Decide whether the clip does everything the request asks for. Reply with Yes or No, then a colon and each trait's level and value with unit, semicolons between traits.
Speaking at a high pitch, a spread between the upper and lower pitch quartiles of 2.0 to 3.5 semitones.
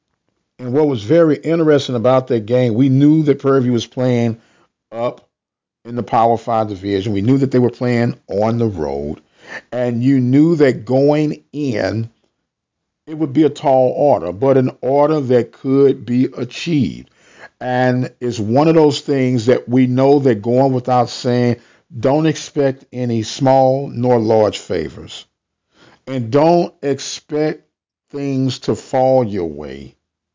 No: low, 130 Hz; average, 2.8 semitones